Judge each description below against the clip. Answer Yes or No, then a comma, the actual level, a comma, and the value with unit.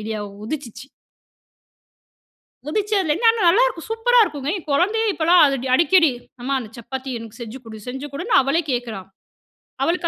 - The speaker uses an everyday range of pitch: No, wide, 6.9 semitones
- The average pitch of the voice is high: Yes, very high, 300 Hz